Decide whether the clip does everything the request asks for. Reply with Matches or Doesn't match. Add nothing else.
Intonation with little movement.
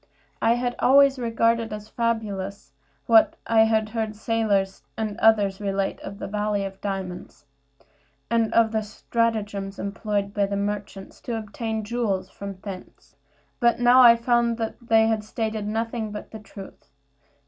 Matches